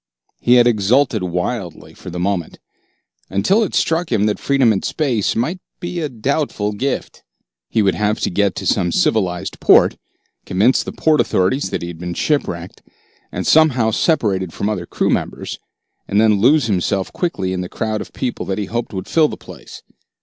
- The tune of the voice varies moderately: No, wide, 6.0 semitones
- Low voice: Yes, low, 110 Hz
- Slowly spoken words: No, average, 185 wpm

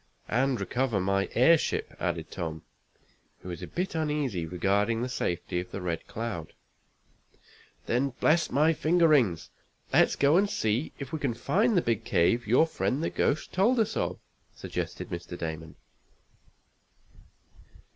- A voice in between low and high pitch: No, low, 120 Hz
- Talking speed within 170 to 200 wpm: No, average, 145 wpm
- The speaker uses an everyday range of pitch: No, wide, 9.0 semitones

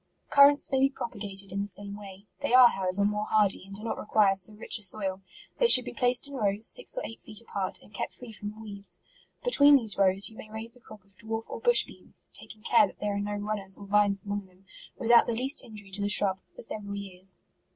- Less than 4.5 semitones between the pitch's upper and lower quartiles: Yes, narrow, 2.5 semitones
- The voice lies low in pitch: No, high, 210 Hz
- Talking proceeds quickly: Yes, fast, 240 wpm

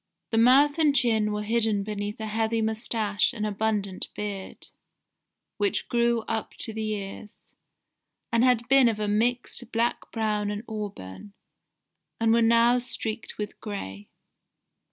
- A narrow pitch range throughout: Yes, narrow, 2.1 semitones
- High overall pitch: Yes, high, 220 Hz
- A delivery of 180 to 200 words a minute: No, average, 140 wpm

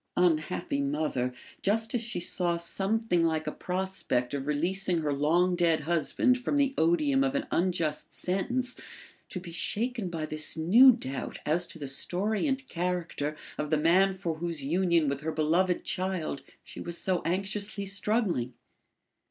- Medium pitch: Yes, medium, 175 Hz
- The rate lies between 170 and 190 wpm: No, average, 160 wpm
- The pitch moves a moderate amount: Yes, average, 4.1 semitones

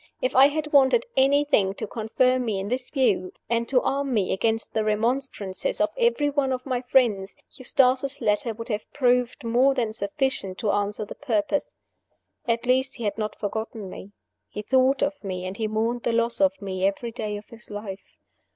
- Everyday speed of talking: Yes, average, 190 wpm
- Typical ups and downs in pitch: Yes, average, 4.1 semitones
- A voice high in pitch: Yes, high, 235 Hz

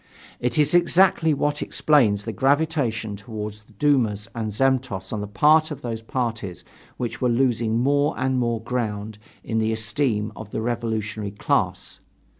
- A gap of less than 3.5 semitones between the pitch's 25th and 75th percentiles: No, average, 3.9 semitones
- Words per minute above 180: No, average, 150 wpm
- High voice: No, low, 115 Hz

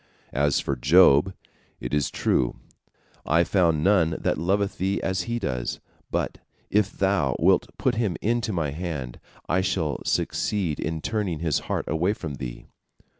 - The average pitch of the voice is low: Yes, very low, 85 Hz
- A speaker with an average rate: Yes, average, 155 wpm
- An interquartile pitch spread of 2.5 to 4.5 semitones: No, average, 5.0 semitones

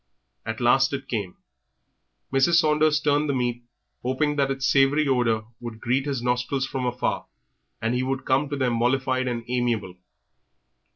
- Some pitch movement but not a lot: No, narrow, 2.3 semitones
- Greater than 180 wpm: No, average, 165 wpm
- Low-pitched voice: Yes, low, 130 Hz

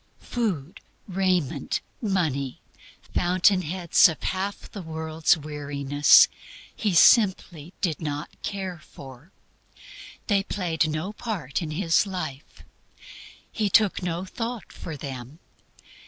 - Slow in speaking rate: Yes, slow, 110 wpm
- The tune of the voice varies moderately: Yes, average, 4.4 semitones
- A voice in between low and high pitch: Yes, medium, 170 Hz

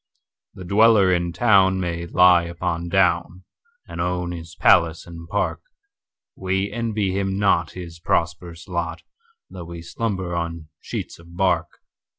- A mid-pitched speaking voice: No, very low, 90 Hz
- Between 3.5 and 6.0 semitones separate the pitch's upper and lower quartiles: No, narrow, 2.5 semitones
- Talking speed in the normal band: No, slow, 125 wpm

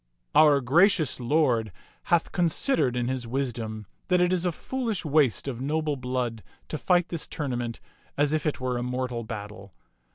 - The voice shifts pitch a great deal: No, average, 4.8 semitones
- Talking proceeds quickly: No, average, 170 wpm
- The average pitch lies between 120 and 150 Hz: Yes, low, 135 Hz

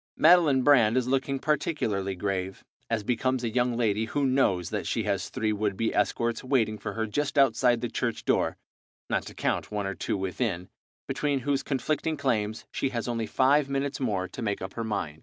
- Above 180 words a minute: Yes, average, 195 wpm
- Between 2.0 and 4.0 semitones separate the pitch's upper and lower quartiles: No, average, 4.6 semitones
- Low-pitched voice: Yes, low, 120 Hz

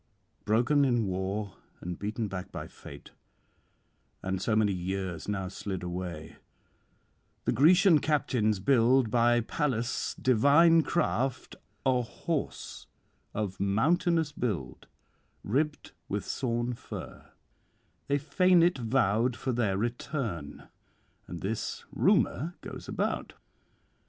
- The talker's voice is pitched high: No, low, 115 Hz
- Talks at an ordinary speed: No, slow, 110 wpm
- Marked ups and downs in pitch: Yes, wide, 6.2 semitones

